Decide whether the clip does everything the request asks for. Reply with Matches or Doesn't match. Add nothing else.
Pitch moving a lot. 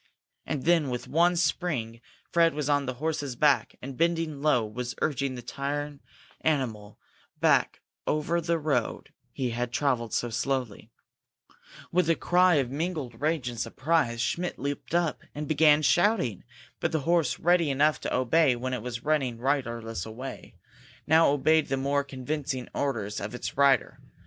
Doesn't match